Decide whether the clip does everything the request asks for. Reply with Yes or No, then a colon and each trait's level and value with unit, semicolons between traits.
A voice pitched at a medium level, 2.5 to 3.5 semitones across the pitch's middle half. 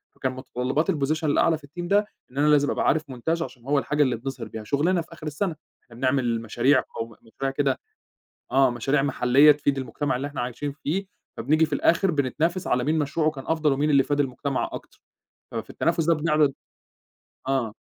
Yes: medium, 145 Hz; average, 3.1 semitones